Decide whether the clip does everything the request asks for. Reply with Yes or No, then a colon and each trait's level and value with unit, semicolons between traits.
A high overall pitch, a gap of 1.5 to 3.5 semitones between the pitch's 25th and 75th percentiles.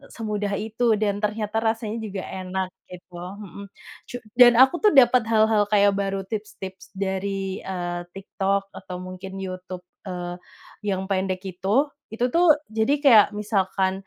Yes: high, 200 Hz; narrow, 2.6 semitones